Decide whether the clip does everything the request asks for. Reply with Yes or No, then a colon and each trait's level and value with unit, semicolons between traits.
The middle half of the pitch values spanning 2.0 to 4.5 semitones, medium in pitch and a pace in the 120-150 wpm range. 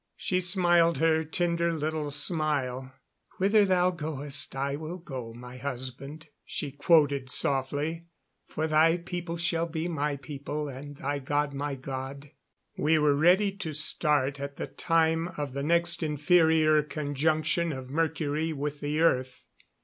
Yes: average, 2.8 semitones; medium, 150 Hz; average, 140 wpm